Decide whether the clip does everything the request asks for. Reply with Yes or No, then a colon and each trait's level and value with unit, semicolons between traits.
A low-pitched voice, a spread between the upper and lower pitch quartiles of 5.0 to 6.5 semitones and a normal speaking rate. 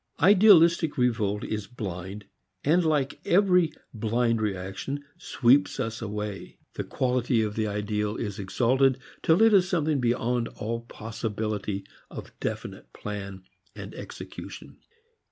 No: low, 115 Hz; wide, 5.5 semitones; slow, 120 wpm